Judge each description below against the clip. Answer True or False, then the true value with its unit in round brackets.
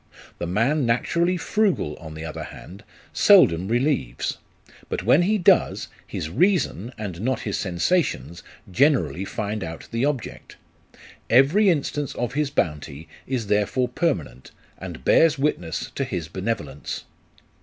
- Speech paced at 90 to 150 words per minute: True (135 wpm)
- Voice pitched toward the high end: False (115 Hz)